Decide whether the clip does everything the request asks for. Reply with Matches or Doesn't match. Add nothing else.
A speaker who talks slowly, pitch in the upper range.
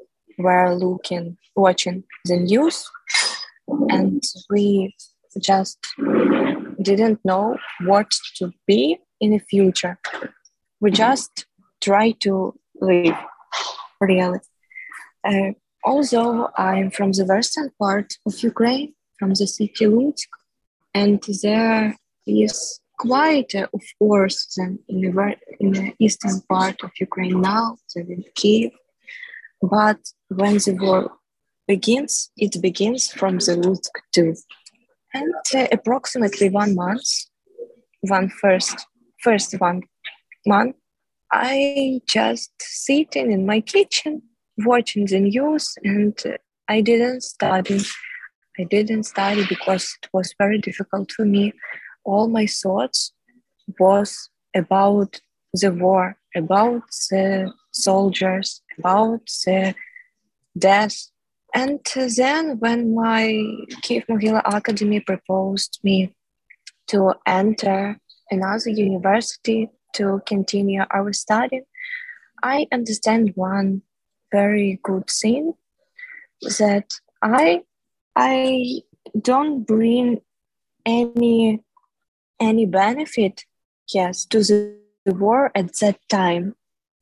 Matches